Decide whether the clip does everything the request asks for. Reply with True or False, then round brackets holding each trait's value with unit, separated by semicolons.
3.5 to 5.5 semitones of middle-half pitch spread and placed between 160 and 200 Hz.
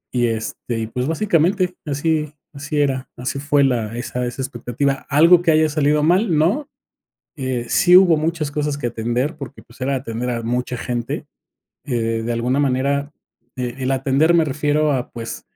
False (3.8 semitones; 140 Hz)